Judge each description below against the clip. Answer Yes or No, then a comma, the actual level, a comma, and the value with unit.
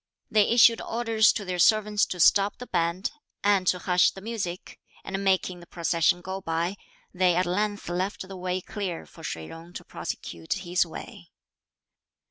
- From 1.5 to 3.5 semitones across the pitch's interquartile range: Yes, average, 2.7 semitones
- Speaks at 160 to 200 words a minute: Yes, average, 170 wpm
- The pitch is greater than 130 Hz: Yes, medium, 185 Hz